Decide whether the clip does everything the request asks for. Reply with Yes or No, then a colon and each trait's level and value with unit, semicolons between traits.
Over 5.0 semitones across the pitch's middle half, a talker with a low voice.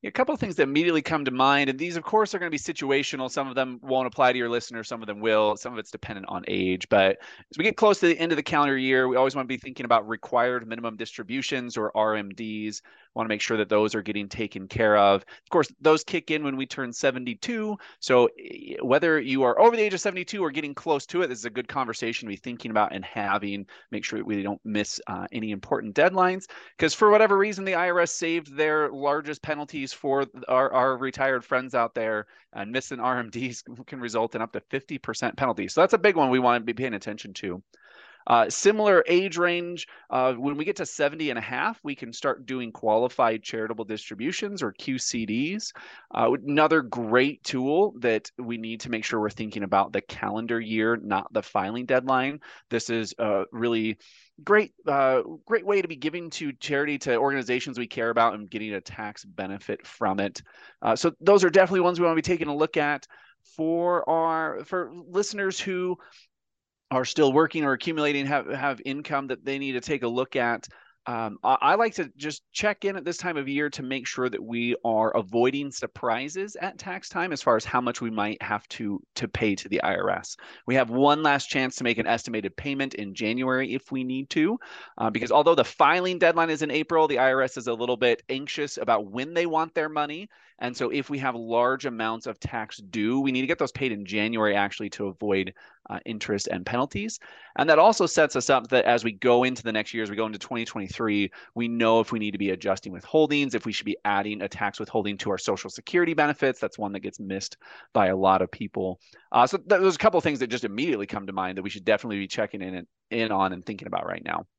Yes: wide, 5.6 semitones; low, 130 Hz